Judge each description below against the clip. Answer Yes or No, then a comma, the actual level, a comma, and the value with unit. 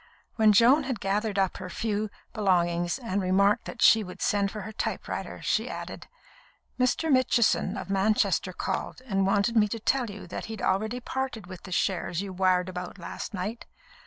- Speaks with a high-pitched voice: Yes, high, 205 Hz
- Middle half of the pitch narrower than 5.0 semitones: Yes, average, 3.2 semitones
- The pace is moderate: Yes, average, 180 wpm